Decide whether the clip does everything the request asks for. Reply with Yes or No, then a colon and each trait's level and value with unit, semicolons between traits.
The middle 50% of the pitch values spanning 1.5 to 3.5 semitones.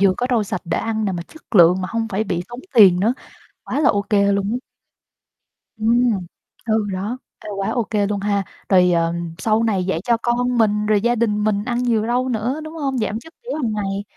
Yes: average, 3.2 semitones